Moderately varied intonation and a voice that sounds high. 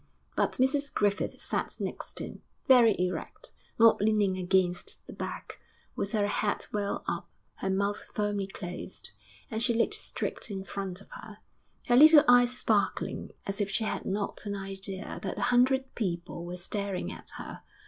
Yes: average, 3.2 semitones; high, 205 Hz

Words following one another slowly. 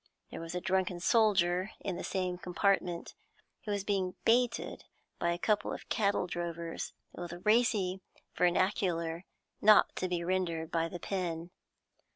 No: average, 145 wpm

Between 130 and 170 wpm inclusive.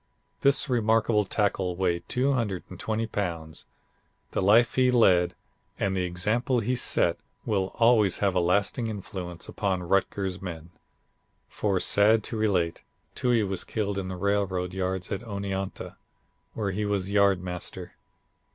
Yes: slow, 135 wpm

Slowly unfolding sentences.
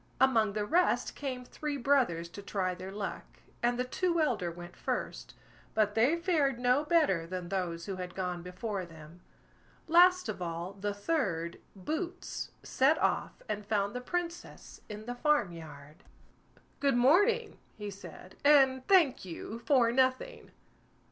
No: average, 150 wpm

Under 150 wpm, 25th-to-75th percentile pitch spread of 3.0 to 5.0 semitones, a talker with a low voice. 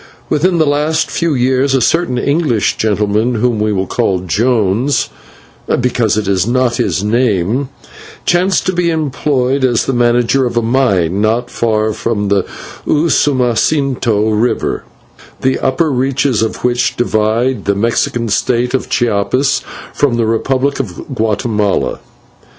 Yes: average, 140 wpm; average, 3.8 semitones; low, 120 Hz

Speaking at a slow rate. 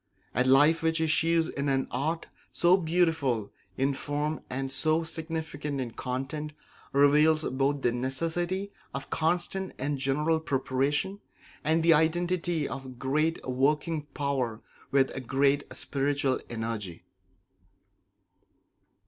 Yes: slow, 115 wpm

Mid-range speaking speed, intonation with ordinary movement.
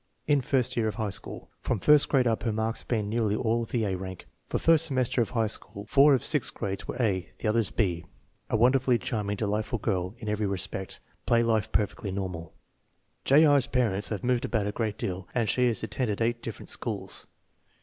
No: fast, 215 wpm; average, 3.4 semitones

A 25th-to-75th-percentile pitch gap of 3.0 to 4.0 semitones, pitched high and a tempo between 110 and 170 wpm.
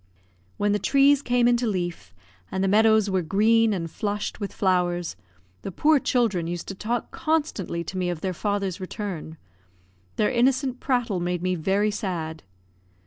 No: average, 4.7 semitones; high, 200 Hz; average, 160 wpm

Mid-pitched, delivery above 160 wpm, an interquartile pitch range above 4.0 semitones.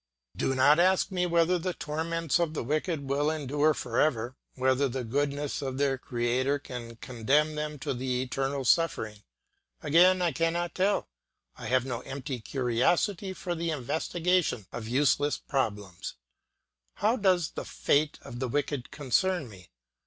No: medium, 145 Hz; average, 155 wpm; average, 4.6 semitones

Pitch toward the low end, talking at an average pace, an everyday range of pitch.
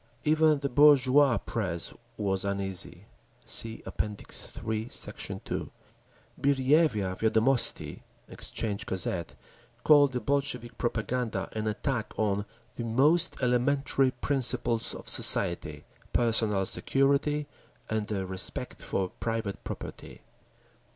No: low, 115 Hz; slow, 100 wpm; average, 4.9 semitones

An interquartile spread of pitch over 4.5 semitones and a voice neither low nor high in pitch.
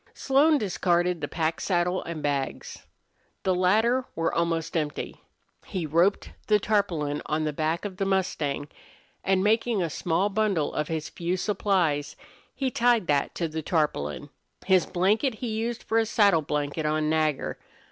Yes: average, 5.0 semitones; medium, 175 Hz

